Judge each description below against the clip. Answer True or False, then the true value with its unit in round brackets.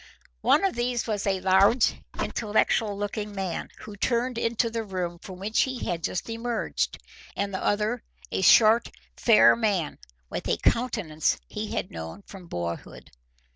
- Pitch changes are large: False (3.6 semitones)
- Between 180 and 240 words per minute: False (155 wpm)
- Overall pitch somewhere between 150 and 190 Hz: False (205 Hz)